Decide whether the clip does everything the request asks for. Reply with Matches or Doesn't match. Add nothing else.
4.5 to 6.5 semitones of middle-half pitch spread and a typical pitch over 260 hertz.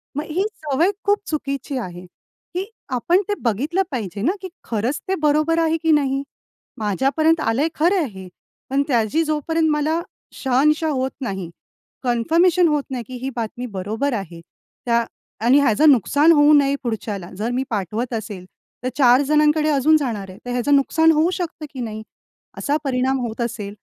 Matches